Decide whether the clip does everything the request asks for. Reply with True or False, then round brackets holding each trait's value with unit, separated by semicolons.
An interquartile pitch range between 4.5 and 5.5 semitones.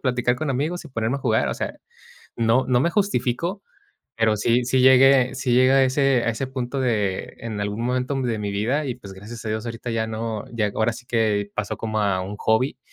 False (3.0 semitones)